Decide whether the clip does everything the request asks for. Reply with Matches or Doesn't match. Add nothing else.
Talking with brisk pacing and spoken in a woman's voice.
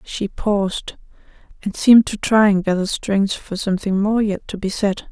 Doesn't match